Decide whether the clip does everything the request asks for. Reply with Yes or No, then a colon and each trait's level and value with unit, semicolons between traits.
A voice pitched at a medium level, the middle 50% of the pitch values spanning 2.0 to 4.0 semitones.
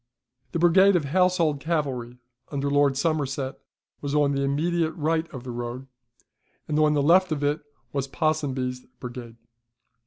Yes: medium, 145 Hz; average, 3.1 semitones